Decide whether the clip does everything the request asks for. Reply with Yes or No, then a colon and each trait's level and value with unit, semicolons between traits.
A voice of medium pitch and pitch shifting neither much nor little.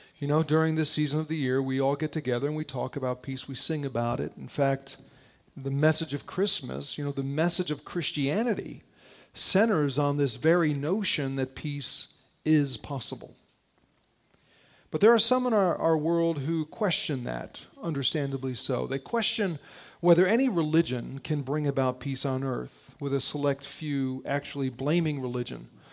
Yes: medium, 145 Hz; average, 3.0 semitones